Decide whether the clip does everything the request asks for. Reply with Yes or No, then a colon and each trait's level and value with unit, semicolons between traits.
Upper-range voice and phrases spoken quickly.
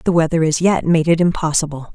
No: medium, 165 Hz; fast, 215 wpm